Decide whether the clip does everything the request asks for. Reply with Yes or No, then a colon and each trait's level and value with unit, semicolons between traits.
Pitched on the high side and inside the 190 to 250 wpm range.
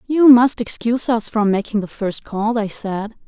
Yes: high, 225 Hz; average, 200 wpm